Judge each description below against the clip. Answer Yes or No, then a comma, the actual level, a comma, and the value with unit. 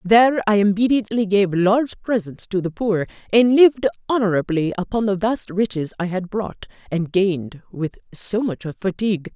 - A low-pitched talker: No, high, 200 Hz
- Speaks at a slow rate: No, average, 160 wpm